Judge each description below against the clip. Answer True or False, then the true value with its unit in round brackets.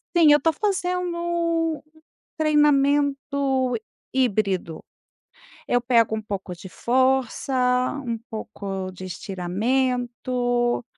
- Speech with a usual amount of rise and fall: True (4.6 semitones)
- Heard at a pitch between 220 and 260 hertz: True (250 Hz)